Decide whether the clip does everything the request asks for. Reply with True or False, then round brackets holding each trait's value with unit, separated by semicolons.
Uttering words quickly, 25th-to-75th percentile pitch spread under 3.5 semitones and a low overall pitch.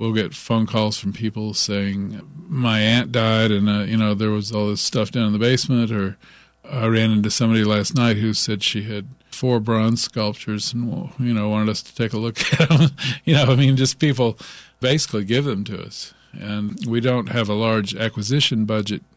True (215 wpm; 2.9 semitones; 110 Hz)